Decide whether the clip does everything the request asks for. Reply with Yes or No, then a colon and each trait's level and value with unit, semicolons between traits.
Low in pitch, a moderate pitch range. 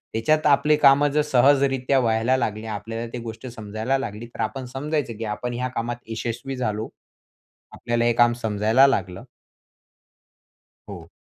Yes: low, 120 Hz; average, 3.2 semitones